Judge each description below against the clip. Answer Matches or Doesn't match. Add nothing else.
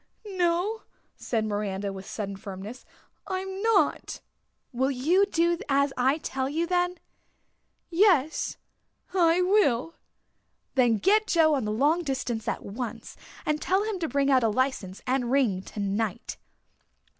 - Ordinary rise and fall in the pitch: Doesn't match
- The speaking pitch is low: Doesn't match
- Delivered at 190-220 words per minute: Doesn't match